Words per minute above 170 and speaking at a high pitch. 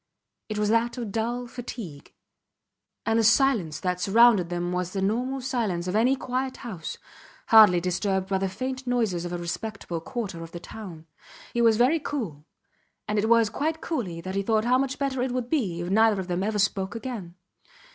Yes: average, 195 wpm; high, 215 Hz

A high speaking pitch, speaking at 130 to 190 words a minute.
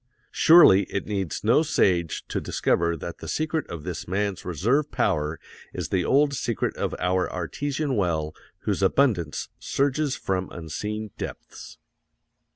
No: low, 100 Hz; average, 140 wpm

